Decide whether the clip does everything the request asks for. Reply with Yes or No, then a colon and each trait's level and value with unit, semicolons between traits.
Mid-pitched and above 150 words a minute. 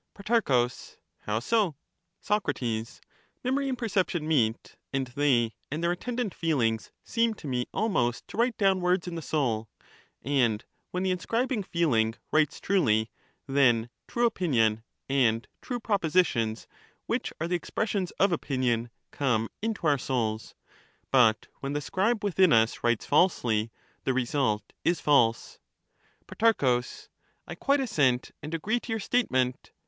No: medium, 145 Hz; average, 145 wpm